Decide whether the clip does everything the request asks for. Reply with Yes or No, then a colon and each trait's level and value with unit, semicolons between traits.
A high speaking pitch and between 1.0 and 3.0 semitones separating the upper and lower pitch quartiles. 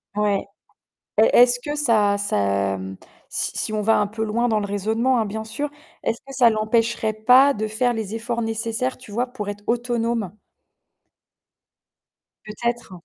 Yes: high, 225 Hz; narrow, 2.4 semitones